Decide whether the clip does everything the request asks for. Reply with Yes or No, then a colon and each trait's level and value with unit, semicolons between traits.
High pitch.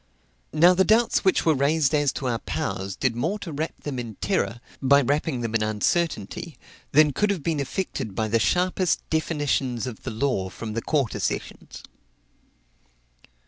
No: medium, 140 Hz